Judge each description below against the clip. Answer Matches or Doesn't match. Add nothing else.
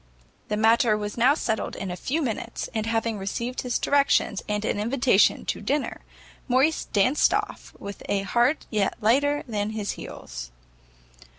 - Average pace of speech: Matches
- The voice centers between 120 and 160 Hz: Doesn't match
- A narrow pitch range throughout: Doesn't match